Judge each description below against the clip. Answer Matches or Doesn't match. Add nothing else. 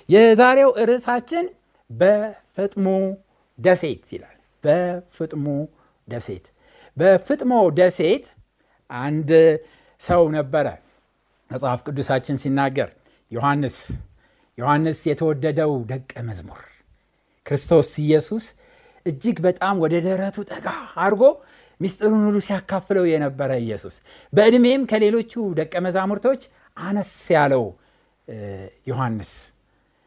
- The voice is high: Doesn't match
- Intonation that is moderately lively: Doesn't match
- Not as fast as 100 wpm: Matches